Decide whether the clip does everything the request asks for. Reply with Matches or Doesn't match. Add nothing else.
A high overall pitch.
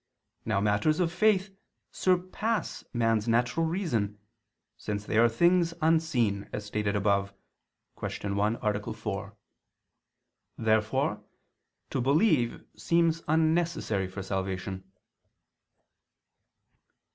Doesn't match